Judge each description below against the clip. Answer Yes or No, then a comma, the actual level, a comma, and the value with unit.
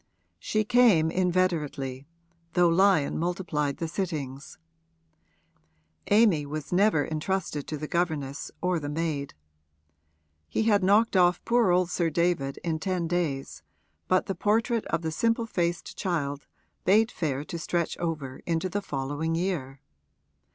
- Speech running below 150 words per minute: Yes, slow, 135 wpm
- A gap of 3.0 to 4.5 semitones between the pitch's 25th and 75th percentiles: Yes, average, 4.0 semitones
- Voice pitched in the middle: Yes, medium, 170 Hz